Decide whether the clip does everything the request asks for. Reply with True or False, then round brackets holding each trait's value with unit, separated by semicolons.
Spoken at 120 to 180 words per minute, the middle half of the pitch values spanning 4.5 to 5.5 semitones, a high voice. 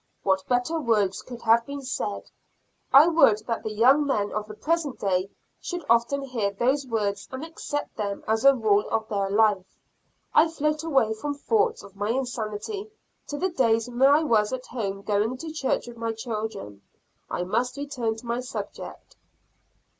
True (175 wpm; 4.9 semitones; 235 Hz)